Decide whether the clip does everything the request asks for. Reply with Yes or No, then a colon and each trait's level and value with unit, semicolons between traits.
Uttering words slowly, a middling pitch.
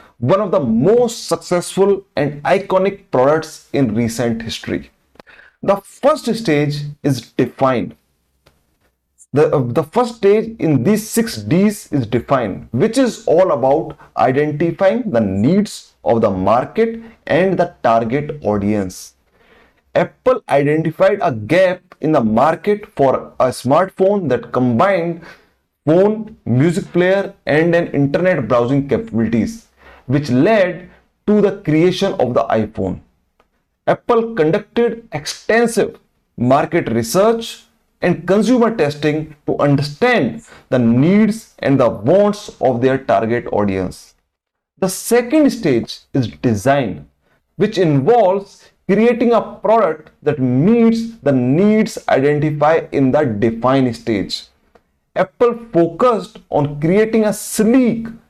Yes: slow, 115 wpm; medium, 175 Hz